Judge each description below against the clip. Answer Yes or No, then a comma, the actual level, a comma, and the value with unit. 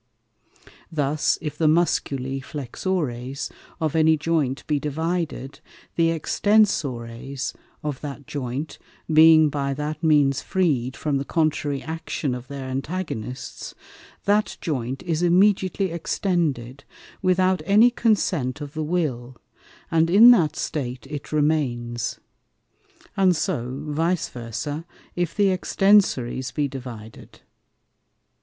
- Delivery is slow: Yes, slow, 110 wpm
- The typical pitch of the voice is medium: Yes, medium, 150 Hz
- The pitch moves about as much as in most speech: Yes, average, 4.4 semitones